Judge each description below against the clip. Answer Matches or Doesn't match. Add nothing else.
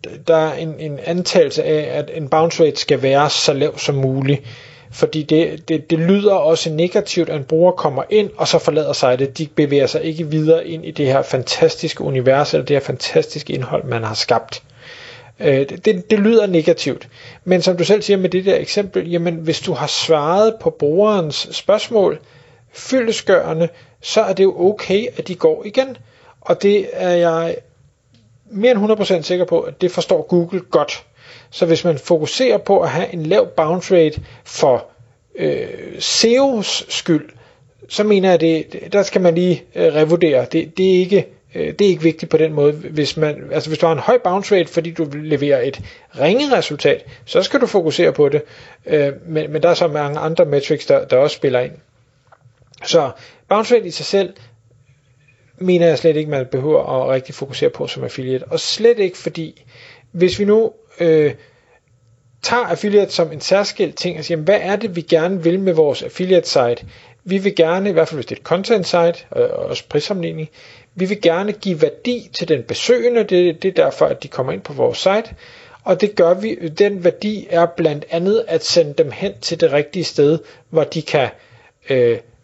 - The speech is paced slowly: Doesn't match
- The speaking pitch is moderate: Matches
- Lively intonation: Doesn't match